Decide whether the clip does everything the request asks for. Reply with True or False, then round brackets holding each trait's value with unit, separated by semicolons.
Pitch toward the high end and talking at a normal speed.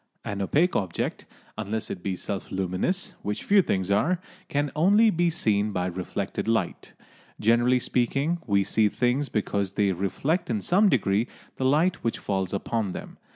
False (110 Hz; 160 wpm)